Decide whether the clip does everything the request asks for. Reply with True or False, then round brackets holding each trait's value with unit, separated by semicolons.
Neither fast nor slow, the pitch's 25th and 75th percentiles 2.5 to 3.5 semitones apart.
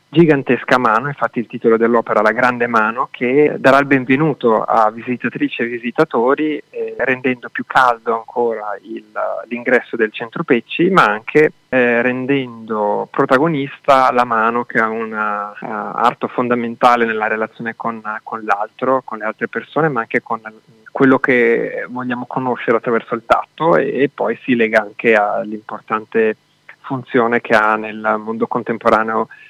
True (145 wpm; 2.8 semitones)